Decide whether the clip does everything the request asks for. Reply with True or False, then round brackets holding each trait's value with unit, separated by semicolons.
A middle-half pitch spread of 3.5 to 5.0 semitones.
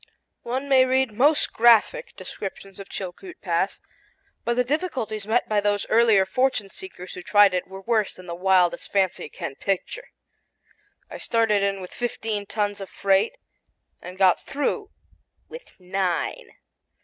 True (4.5 semitones)